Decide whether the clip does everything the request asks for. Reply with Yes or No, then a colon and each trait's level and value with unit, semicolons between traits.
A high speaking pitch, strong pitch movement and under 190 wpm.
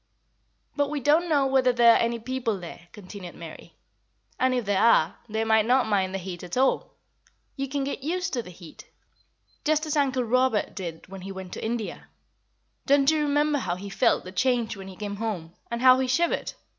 No: high, 235 Hz; wide, 5.8 semitones; fast, 205 wpm